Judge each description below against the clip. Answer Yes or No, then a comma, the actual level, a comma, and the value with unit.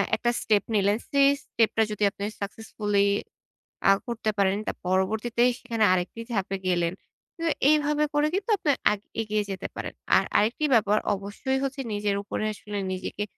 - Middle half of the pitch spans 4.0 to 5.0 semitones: No, average, 3.3 semitones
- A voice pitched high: Yes, high, 210 Hz